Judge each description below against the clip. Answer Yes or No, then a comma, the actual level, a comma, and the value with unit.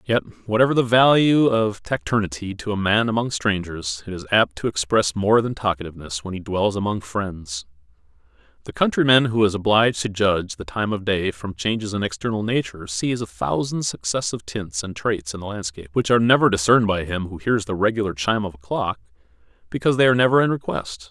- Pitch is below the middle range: Yes, low, 105 Hz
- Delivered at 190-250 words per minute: Yes, average, 200 wpm